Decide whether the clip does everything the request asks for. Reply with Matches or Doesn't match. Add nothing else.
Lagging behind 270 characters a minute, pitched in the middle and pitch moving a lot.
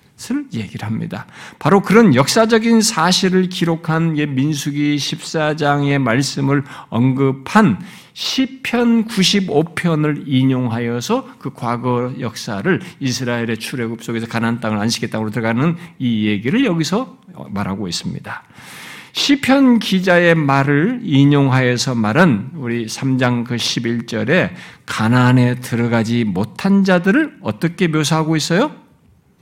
Matches